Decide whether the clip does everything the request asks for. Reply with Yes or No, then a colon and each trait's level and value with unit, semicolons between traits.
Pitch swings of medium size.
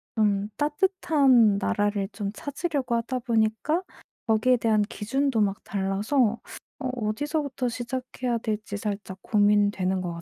Yes: average, 4.2 semitones